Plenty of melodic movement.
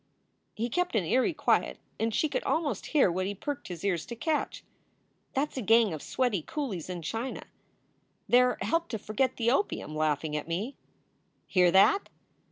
Yes: wide, 6.7 semitones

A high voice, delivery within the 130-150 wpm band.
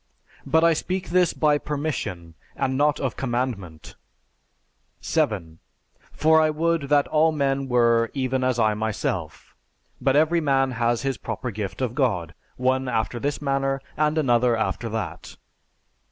No: low, 130 Hz; average, 145 wpm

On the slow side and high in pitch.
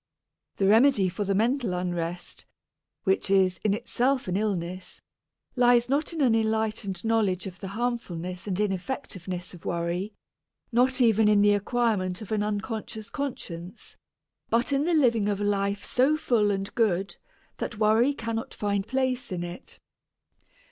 No: average, 150 wpm; high, 210 Hz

